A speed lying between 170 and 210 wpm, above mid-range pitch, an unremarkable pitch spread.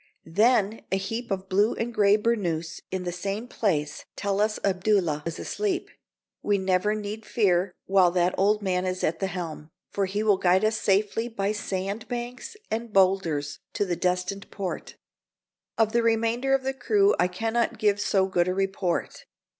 Yes: average, 180 wpm; high, 200 Hz; average, 3.3 semitones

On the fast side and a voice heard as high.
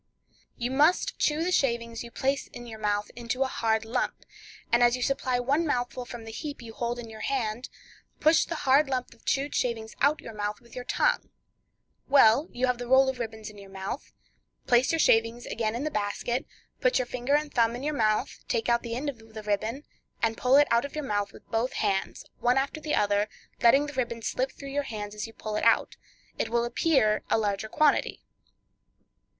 Yes: fast, 215 wpm; high, 240 Hz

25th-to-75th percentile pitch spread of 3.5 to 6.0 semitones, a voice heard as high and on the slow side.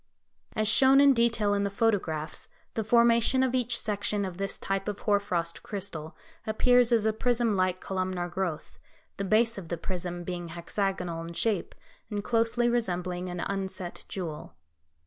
No: average, 4.3 semitones; high, 200 Hz; average, 165 wpm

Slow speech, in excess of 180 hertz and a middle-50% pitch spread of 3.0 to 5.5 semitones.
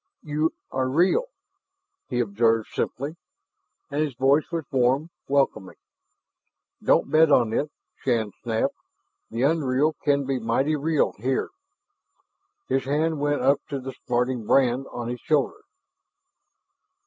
No: slow, 125 wpm; low, 135 Hz; average, 3.3 semitones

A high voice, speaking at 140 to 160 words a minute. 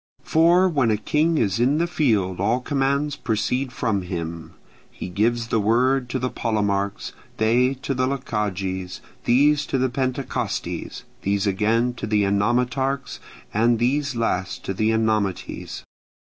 No: low, 120 Hz; average, 145 wpm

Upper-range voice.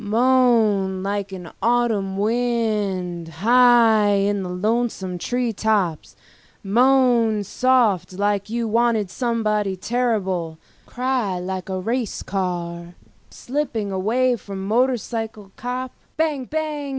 Yes: high, 215 Hz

